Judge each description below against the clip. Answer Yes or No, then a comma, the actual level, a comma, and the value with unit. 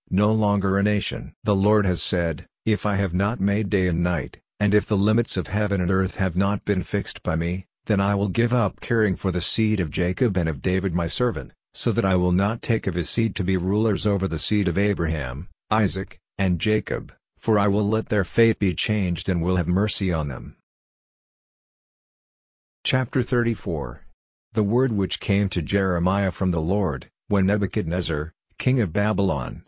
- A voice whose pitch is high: No, low, 100 Hz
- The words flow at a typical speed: Yes, average, 195 wpm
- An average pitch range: Yes, average, 3.1 semitones